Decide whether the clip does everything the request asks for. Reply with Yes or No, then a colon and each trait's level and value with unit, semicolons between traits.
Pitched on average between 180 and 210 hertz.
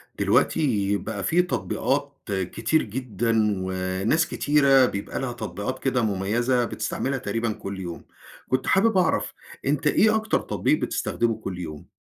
No: low, 120 Hz